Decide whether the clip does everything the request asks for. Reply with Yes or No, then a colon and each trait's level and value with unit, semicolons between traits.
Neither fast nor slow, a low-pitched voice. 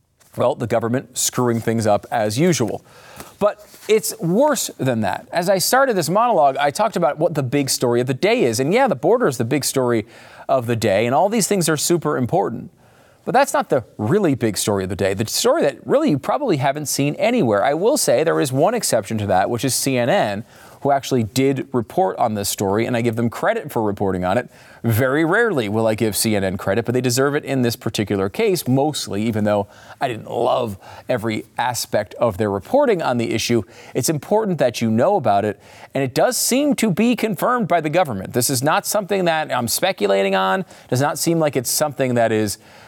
No: fast, 220 wpm; low, 125 Hz